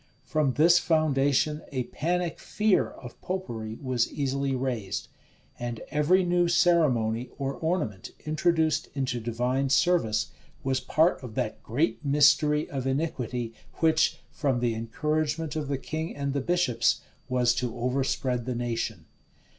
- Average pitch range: Yes, average, 4.4 semitones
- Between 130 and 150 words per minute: Yes, slow, 135 wpm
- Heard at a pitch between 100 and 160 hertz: Yes, medium, 140 Hz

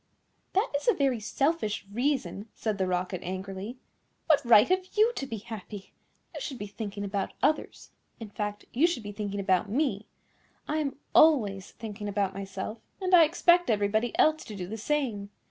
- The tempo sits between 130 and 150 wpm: No, average, 180 wpm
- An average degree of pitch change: No, wide, 6.2 semitones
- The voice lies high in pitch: Yes, high, 215 Hz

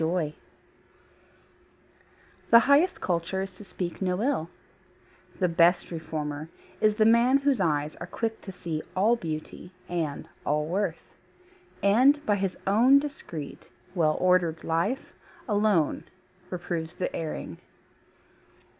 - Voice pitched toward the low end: No, medium, 180 Hz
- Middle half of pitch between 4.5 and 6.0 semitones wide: Yes, average, 5.0 semitones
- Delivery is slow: Yes, slow, 125 wpm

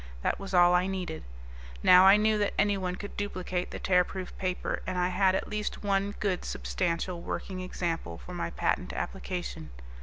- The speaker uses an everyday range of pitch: No, narrow, 1.8 semitones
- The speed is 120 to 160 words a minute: No, average, 175 wpm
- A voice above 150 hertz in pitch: Yes, medium, 185 Hz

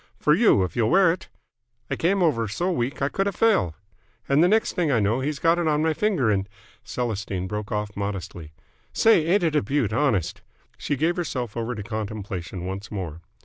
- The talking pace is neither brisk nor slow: No, fast, 210 wpm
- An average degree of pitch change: No, wide, 8.4 semitones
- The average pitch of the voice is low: Yes, low, 120 Hz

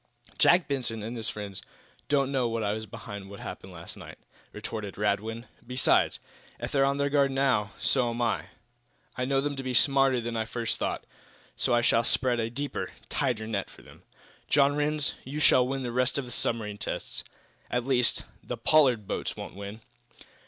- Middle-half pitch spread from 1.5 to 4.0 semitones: Yes, average, 3.5 semitones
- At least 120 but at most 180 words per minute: No, average, 190 wpm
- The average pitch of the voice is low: Yes, low, 120 Hz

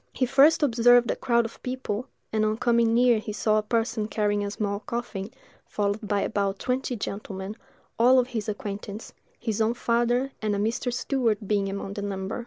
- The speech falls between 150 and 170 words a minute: No, average, 190 wpm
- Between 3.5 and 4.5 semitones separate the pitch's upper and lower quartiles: No, average, 2.8 semitones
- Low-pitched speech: No, high, 220 Hz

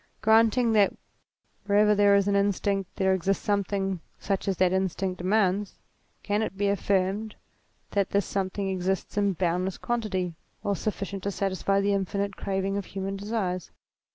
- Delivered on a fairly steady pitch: Yes, narrow, 1.2 semitones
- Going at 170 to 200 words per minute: No, average, 155 wpm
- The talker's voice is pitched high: Yes, high, 195 Hz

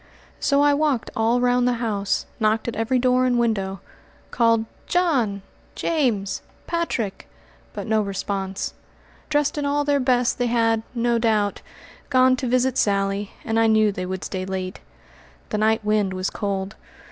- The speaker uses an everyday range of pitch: Yes, average, 4.0 semitones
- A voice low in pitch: No, high, 225 Hz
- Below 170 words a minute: Yes, average, 160 wpm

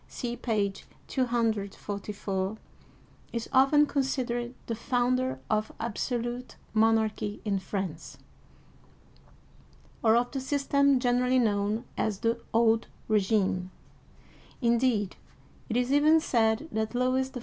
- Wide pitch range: No, average, 3.0 semitones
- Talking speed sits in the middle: No, slow, 105 wpm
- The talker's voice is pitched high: Yes, high, 235 Hz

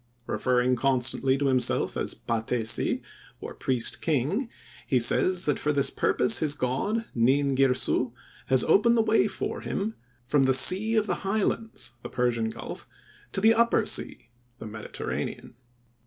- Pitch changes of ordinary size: No, wide, 8.0 semitones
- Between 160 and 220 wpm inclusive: No, average, 140 wpm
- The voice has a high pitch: No, low, 135 Hz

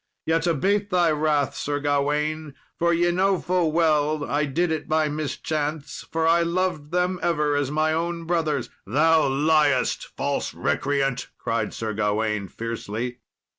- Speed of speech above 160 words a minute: No, average, 145 wpm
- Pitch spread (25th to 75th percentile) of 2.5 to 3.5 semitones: Yes, average, 2.8 semitones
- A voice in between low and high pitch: Yes, medium, 155 Hz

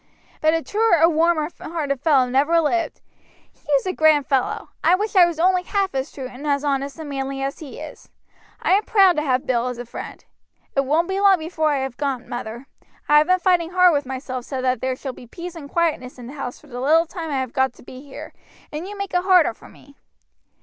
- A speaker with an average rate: No, fast, 240 wpm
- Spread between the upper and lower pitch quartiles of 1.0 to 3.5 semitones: No, average, 4.5 semitones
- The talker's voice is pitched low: No, very high, 295 Hz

